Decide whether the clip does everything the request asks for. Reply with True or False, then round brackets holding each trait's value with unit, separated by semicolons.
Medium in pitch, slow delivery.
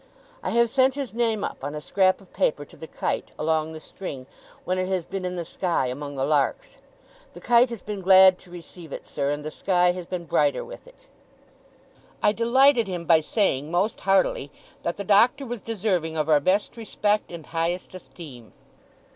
False (180 Hz; 195 wpm)